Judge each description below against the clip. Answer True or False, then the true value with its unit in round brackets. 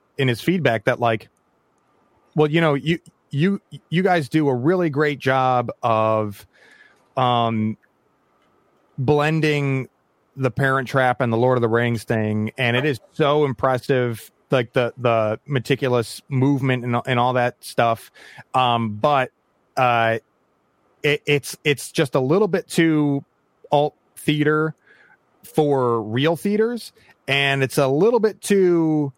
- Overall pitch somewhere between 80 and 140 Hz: True (135 Hz)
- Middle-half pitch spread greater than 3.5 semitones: True (4.0 semitones)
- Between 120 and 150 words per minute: True (140 wpm)